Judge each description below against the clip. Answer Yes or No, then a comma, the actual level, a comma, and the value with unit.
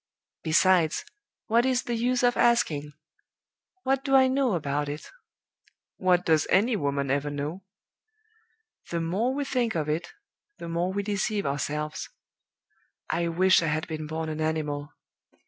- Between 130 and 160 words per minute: Yes, average, 145 wpm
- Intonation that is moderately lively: No, wide, 7.2 semitones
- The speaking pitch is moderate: Yes, medium, 170 Hz